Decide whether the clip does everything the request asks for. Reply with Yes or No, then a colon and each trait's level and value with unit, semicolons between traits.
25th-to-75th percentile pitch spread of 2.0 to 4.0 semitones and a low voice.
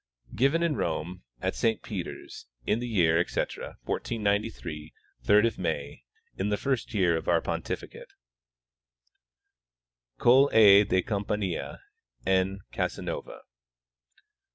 No: average, 4.5 semitones; low, 100 Hz